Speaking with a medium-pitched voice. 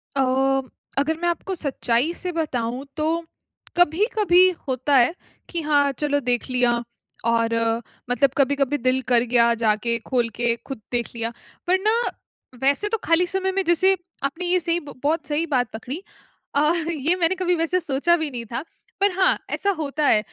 No: very high, 285 Hz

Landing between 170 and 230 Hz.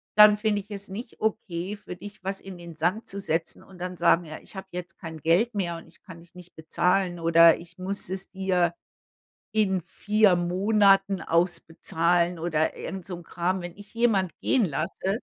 Yes: medium, 185 Hz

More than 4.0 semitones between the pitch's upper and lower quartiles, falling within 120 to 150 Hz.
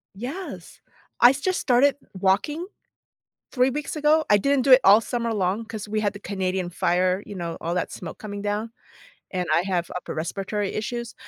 No: average, 5.0 semitones; high, 210 Hz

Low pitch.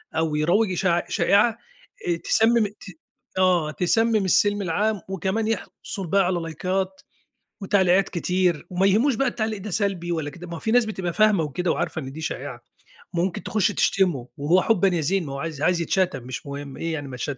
No: medium, 180 Hz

